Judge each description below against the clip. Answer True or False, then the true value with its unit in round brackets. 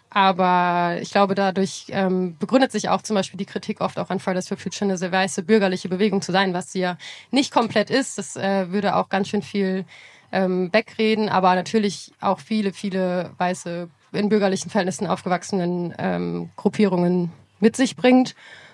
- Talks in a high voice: True (195 Hz)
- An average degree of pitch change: False (2.3 semitones)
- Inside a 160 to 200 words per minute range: True (165 wpm)